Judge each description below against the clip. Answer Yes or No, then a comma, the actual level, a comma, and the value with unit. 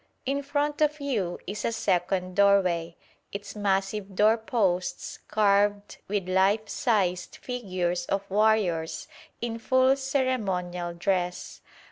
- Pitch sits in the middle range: No, high, 200 Hz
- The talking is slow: Yes, slow, 115 wpm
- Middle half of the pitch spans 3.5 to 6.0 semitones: Yes, average, 3.8 semitones